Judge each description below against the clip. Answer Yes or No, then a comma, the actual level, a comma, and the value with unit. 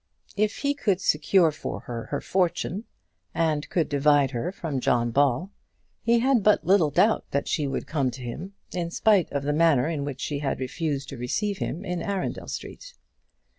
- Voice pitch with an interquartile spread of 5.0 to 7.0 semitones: Yes, wide, 5.6 semitones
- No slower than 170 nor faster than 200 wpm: Yes, average, 185 wpm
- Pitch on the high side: No, medium, 160 Hz